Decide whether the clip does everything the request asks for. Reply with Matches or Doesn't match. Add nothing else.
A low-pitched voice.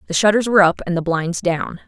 Doesn't match